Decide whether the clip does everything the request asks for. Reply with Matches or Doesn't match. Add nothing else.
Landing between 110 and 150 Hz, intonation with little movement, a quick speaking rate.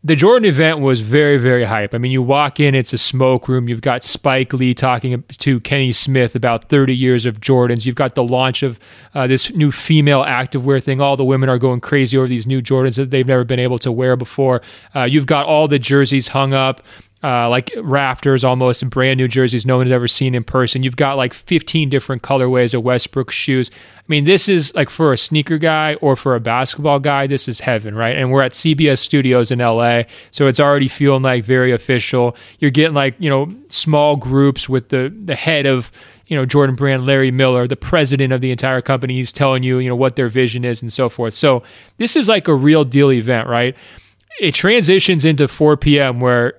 Matches